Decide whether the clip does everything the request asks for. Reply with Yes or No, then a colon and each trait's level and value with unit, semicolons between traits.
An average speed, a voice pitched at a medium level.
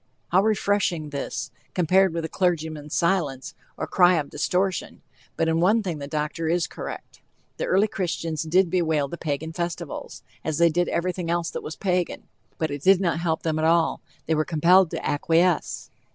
Yes: average, 180 wpm; medium, 170 Hz